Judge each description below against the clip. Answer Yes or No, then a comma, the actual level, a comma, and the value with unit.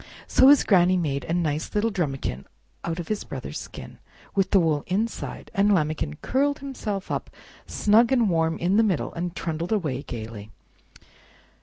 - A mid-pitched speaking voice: Yes, medium, 180 Hz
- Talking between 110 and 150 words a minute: No, average, 165 wpm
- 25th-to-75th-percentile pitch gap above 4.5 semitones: Yes, average, 5.3 semitones